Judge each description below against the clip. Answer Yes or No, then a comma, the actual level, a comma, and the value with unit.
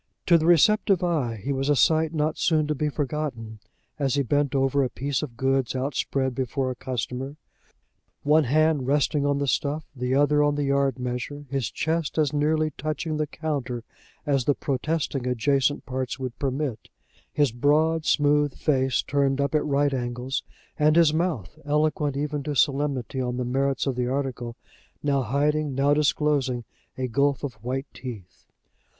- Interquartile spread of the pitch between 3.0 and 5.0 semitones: No, narrow, 2.5 semitones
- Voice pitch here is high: No, medium, 140 Hz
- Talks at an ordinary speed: Yes, average, 170 wpm